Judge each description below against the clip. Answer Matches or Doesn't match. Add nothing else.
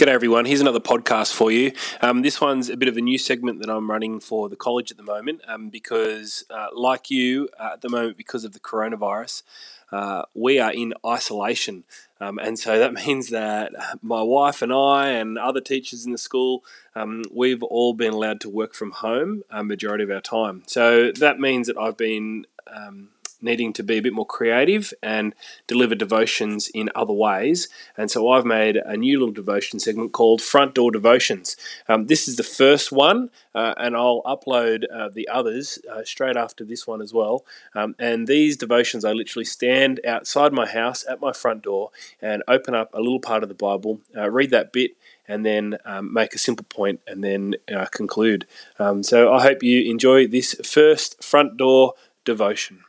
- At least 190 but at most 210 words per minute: Matches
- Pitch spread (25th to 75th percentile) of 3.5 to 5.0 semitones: Doesn't match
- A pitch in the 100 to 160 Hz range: Matches